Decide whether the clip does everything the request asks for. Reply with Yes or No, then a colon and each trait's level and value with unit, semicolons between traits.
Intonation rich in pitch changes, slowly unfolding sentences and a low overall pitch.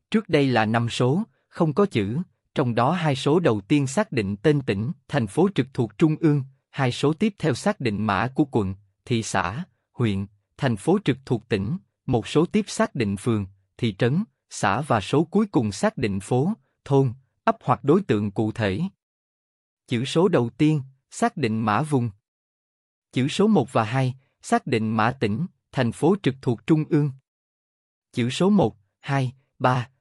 No: wide, 5.7 semitones; average, 185 wpm; low, 130 Hz